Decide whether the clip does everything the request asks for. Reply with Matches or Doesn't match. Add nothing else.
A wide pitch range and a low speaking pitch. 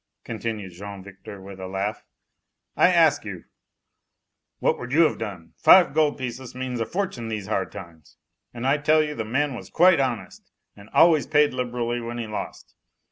Matches